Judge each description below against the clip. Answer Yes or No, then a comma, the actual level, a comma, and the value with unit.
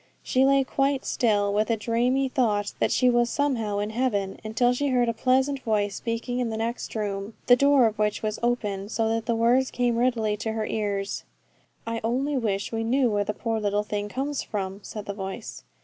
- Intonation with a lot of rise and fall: No, average, 3.1 semitones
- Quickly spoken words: Yes, fast, 210 wpm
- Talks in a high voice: Yes, high, 230 Hz